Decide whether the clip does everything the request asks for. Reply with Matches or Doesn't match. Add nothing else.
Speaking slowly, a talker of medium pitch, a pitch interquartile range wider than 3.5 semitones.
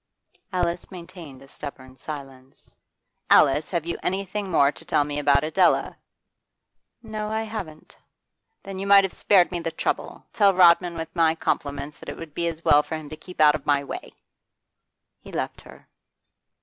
Doesn't match